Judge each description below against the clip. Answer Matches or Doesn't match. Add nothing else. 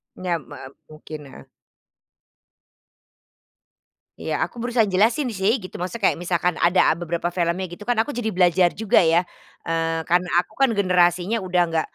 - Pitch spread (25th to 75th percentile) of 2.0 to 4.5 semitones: Matches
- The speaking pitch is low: Doesn't match